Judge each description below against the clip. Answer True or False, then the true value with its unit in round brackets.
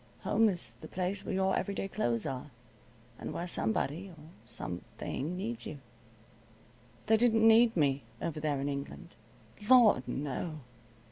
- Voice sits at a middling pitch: True (175 Hz)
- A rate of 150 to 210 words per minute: False (140 wpm)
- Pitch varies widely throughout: True (6.5 semitones)